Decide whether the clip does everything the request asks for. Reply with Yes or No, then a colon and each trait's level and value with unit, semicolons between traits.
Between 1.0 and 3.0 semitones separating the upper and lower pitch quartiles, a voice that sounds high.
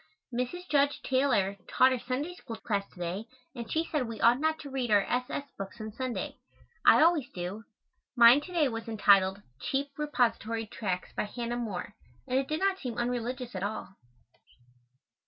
No: average, 4.5 semitones; high, 240 Hz